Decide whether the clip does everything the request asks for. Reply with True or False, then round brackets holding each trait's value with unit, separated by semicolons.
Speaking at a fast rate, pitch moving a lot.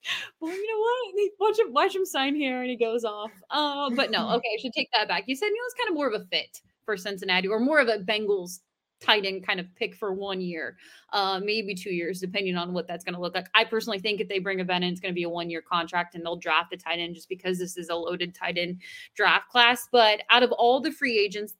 True (270 wpm; 5.7 semitones)